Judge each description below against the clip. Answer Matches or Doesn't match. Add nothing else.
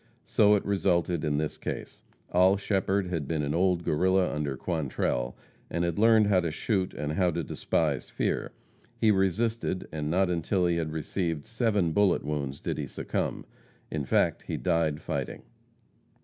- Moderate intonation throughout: Matches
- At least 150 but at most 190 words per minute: Matches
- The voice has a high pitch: Doesn't match